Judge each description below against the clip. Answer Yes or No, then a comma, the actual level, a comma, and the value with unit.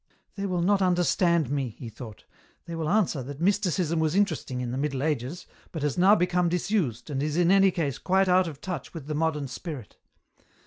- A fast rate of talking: Yes, fast, 215 wpm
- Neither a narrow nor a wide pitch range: Yes, average, 4.4 semitones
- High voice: No, medium, 165 Hz